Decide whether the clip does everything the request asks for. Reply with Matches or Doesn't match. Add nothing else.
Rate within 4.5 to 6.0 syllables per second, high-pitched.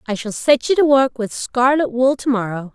Matches